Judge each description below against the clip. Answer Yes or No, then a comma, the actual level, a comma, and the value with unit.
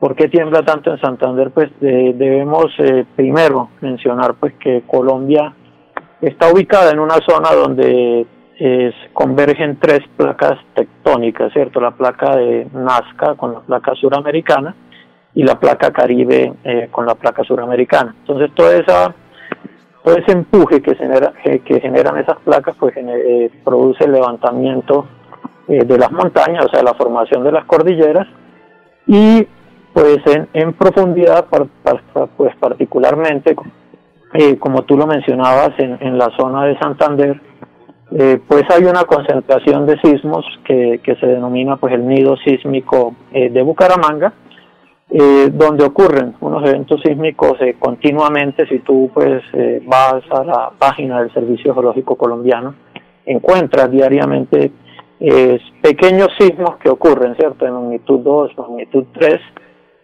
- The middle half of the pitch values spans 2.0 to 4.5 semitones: Yes, average, 3.5 semitones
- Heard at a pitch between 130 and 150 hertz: Yes, low, 135 Hz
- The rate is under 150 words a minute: Yes, average, 135 wpm